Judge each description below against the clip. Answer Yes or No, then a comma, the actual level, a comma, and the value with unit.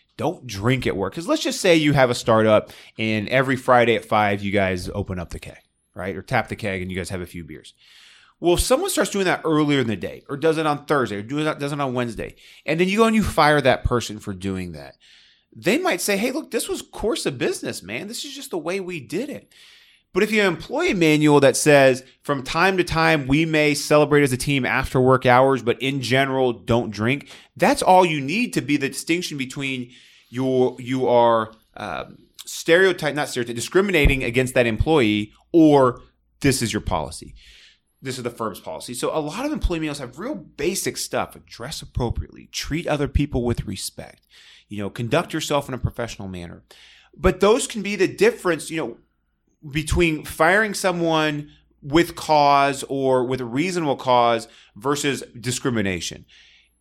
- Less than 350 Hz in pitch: Yes, low, 135 Hz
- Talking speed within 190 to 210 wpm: Yes, average, 200 wpm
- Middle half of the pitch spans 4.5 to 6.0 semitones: Yes, wide, 5.4 semitones